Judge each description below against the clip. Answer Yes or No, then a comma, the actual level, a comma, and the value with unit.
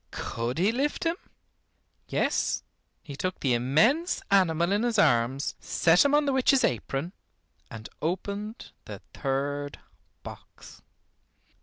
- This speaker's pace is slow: Yes, slow, 125 wpm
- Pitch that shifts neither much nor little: No, wide, 8.9 semitones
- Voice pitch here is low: No, medium, 175 Hz